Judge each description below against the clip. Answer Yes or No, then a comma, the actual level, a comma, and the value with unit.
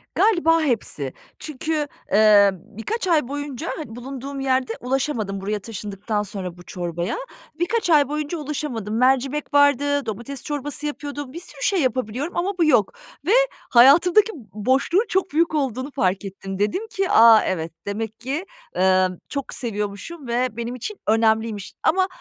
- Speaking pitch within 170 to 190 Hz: No, very high, 260 Hz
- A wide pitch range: Yes, wide, 6.2 semitones